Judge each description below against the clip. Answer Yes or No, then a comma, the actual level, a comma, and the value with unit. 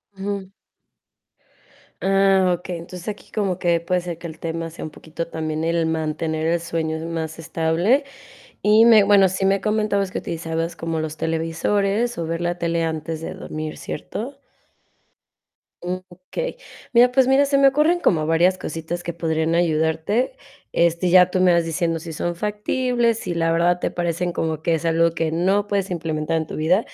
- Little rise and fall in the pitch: No, average, 3.2 semitones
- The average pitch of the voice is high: No, medium, 170 Hz